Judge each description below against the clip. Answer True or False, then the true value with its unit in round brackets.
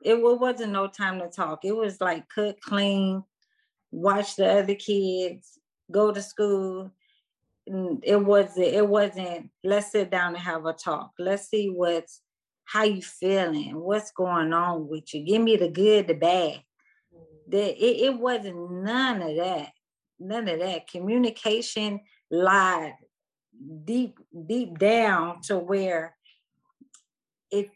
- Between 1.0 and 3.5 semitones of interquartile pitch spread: True (3.2 semitones)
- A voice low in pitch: False (195 Hz)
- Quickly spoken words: False (135 wpm)